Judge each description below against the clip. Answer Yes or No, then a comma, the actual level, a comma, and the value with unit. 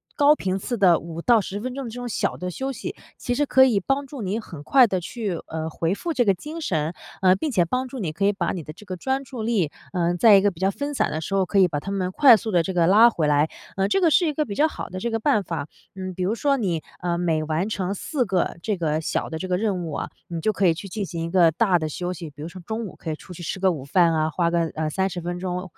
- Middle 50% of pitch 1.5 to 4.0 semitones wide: No, average, 4.9 semitones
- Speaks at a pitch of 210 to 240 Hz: No, high, 190 Hz